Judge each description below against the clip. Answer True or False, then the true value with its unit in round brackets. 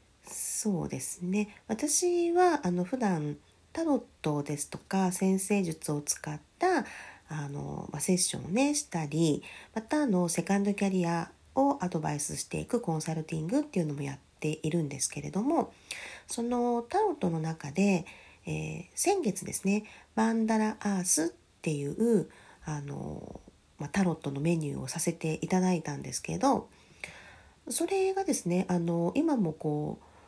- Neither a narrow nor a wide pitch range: False (6.2 semitones)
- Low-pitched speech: False (180 Hz)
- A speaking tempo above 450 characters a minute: False (300 characters per minute)